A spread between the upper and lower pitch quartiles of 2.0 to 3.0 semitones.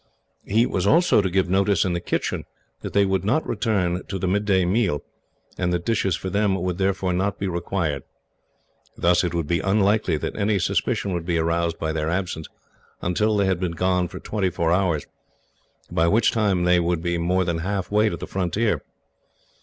Yes: narrow, 2.6 semitones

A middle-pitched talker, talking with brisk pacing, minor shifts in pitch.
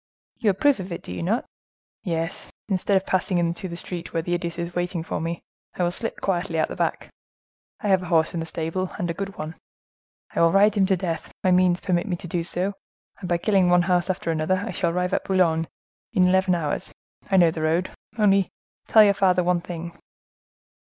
Yes: medium, 180 Hz; fast, 225 wpm; narrow, 2.0 semitones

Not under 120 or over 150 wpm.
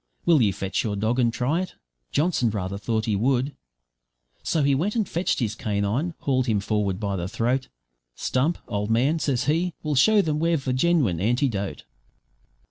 No: average, 180 wpm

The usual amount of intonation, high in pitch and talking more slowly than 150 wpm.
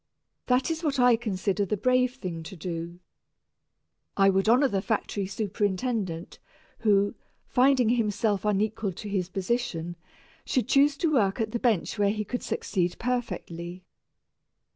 Yes: average, 4.5 semitones; high, 210 Hz; average, 140 wpm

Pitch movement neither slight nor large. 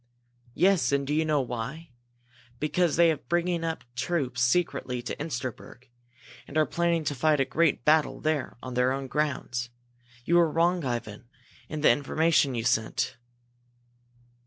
Yes: average, 4.5 semitones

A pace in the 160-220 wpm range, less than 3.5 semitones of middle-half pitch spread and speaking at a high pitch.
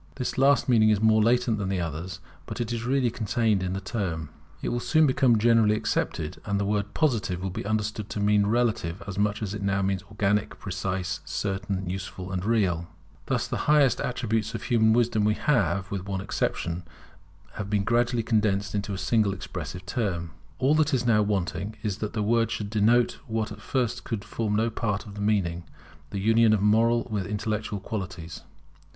No: average, 190 wpm; average, 2.9 semitones; low, 105 Hz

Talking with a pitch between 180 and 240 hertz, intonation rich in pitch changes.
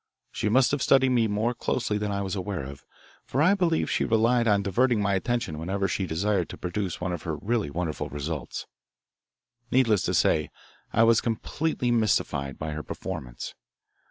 No: low, 105 Hz; wide, 5.7 semitones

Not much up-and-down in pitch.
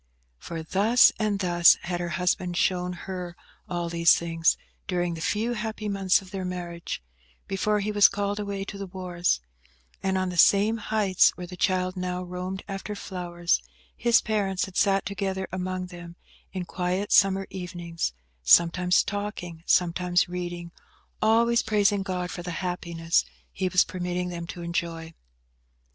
Yes: narrow, 2.1 semitones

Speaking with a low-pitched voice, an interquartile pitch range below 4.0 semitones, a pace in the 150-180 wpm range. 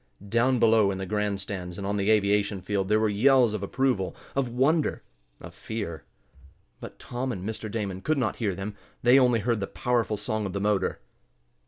No: low, 105 Hz; average, 3.4 semitones; average, 195 wpm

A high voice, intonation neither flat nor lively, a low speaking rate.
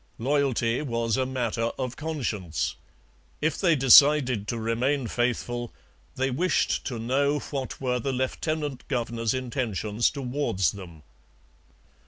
No: low, 125 Hz; average, 3.3 semitones; slow, 120 wpm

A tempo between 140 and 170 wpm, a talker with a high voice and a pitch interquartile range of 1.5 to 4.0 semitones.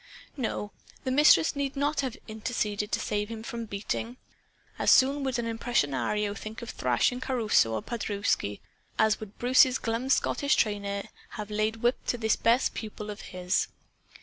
Yes: average, 160 wpm; high, 220 Hz; average, 3.3 semitones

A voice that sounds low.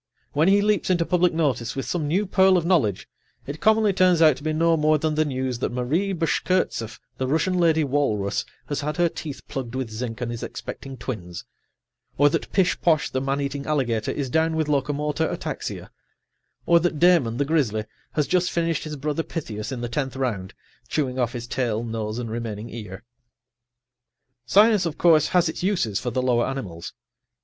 No: medium, 145 Hz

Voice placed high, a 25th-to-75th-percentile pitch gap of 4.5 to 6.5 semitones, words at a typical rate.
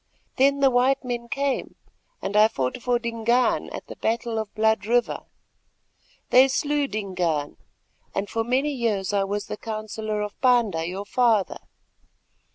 No: high, 225 Hz; average, 3.4 semitones; average, 155 wpm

